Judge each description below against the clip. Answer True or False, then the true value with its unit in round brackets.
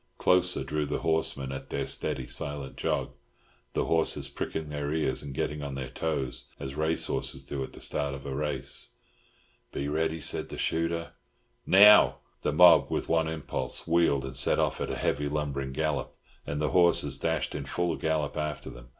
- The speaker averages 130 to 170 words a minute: False (185 wpm)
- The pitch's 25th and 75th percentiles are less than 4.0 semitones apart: True (2.9 semitones)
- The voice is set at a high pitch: False (75 Hz)